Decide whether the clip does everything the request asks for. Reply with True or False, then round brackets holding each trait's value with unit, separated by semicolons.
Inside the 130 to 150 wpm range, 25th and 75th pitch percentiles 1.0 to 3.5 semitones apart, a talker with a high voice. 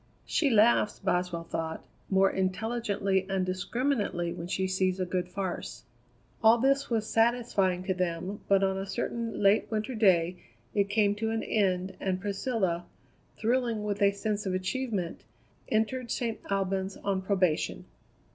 True (145 wpm; 3.2 semitones; 195 Hz)